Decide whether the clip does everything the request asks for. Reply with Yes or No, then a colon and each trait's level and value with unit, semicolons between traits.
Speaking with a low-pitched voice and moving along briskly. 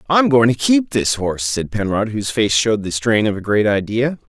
Yes: low, 115 Hz; fast, 235 wpm